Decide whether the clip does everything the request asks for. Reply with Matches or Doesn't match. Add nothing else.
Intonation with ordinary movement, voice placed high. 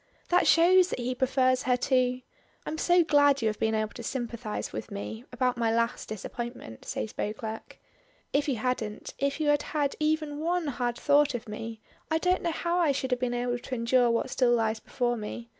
Matches